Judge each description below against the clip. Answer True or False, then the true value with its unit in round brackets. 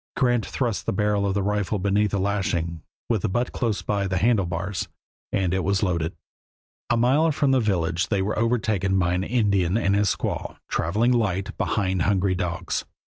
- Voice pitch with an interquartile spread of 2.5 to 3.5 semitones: True (2.9 semitones)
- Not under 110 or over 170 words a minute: False (185 wpm)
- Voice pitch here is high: False (100 Hz)